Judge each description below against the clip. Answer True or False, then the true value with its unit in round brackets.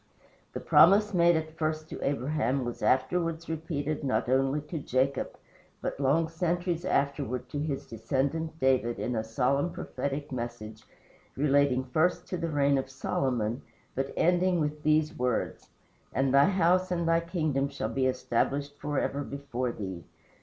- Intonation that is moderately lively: True (3.8 semitones)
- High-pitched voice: False (140 Hz)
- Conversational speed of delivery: True (150 wpm)